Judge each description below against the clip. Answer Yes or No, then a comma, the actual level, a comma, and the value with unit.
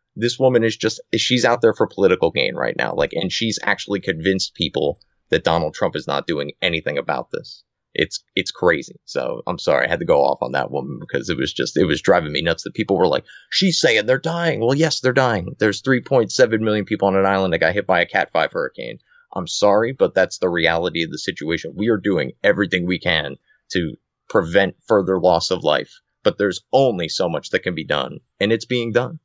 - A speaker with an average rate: No, fast, 230 wpm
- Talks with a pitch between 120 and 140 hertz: No, low, 110 Hz